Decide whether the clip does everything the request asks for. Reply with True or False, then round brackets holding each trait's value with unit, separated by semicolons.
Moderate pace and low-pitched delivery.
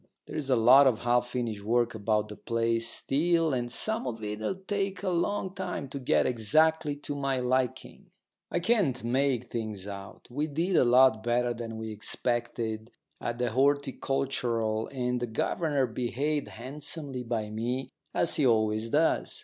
True (160 wpm; 125 Hz)